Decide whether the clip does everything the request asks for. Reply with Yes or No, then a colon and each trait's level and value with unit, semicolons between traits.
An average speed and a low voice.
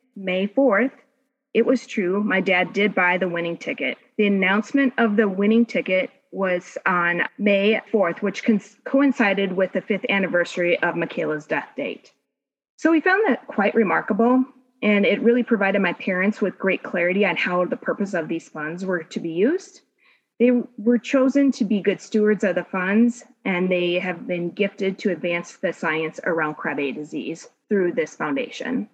No: average, 170 wpm; high, 205 Hz